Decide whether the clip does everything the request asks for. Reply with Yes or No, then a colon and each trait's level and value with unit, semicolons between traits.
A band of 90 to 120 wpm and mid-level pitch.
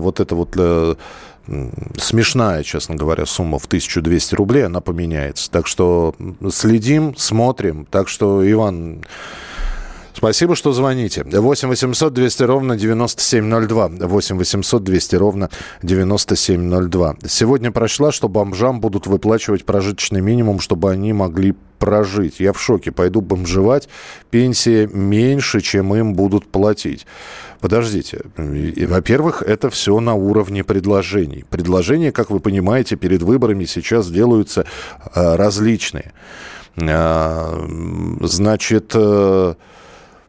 No: slow, 110 wpm; low, 100 Hz